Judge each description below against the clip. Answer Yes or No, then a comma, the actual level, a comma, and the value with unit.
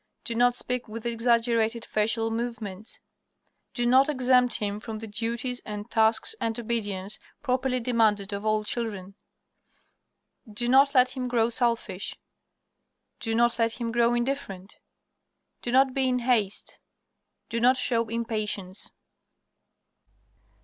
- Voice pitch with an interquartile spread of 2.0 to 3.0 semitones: Yes, narrow, 2.4 semitones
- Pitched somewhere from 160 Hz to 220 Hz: No, high, 230 Hz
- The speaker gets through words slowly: Yes, slow, 130 wpm